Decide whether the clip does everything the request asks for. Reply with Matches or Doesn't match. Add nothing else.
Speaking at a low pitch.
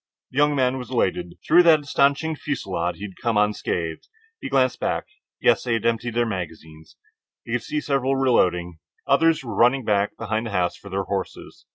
Matches